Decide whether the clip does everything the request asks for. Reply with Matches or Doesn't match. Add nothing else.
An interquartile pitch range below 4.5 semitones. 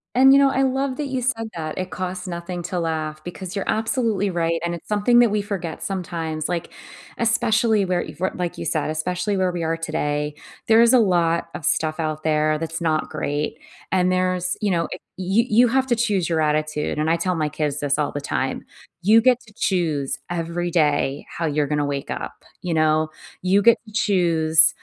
Doesn't match